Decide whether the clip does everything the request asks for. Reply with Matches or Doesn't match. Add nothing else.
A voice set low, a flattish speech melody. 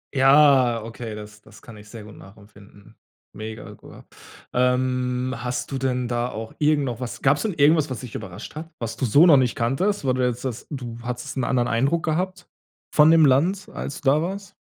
Doesn't match